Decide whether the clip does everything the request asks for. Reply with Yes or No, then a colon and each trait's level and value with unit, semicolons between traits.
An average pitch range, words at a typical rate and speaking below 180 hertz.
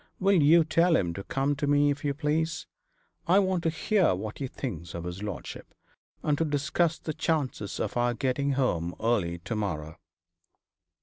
No: wide, 7.9 semitones; average, 180 wpm; medium, 140 Hz